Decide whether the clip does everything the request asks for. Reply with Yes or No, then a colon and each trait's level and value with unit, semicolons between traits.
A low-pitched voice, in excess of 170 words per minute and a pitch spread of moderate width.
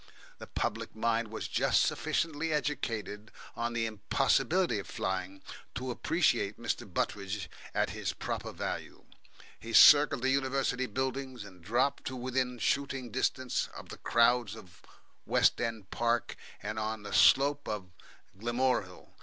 No: low, 120 Hz; slow, 135 wpm; average, 3.8 semitones